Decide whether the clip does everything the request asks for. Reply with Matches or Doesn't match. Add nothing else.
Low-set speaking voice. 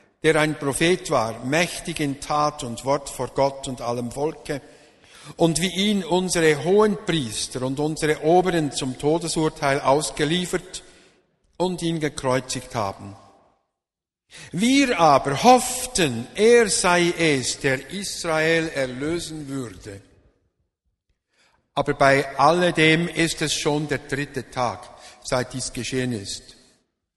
Doesn't match